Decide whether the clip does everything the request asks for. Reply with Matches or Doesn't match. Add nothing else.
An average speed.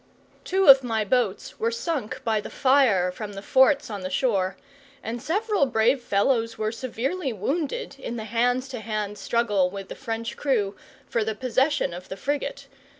Matches